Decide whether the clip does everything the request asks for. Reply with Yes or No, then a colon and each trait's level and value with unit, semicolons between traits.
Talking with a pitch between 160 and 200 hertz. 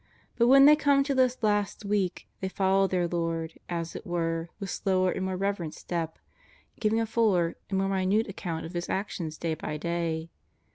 Yes: high, 190 Hz